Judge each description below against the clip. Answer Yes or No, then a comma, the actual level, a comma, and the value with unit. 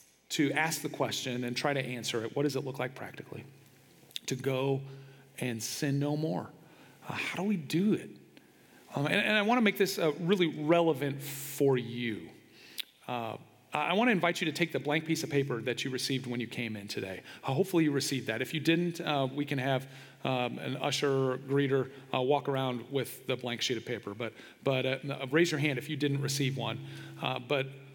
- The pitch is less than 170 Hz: Yes, low, 135 Hz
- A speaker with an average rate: No, fast, 215 wpm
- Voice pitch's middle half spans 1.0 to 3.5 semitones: Yes, average, 2.9 semitones